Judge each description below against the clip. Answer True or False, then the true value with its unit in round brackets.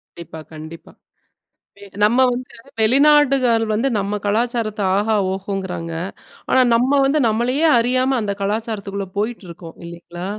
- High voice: True (220 Hz)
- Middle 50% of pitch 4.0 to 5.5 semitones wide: True (4.3 semitones)